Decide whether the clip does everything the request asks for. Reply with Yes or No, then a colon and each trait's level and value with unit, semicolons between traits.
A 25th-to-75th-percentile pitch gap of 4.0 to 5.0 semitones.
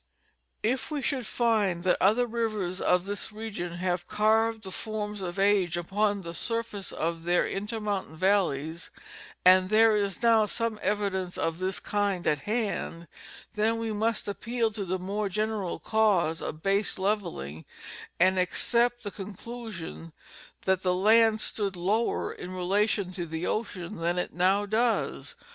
No: average, 3.3 semitones